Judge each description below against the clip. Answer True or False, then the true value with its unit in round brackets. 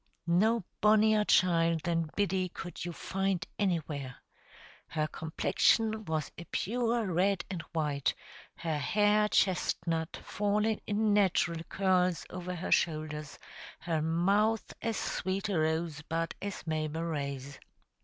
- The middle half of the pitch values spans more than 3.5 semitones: True (4.2 semitones)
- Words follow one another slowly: True (125 wpm)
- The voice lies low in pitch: False (175 Hz)